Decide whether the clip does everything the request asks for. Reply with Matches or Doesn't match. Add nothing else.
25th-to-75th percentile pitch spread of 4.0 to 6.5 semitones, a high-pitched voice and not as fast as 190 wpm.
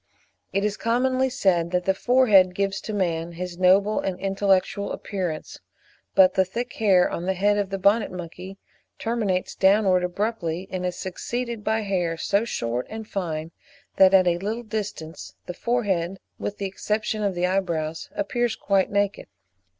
Doesn't match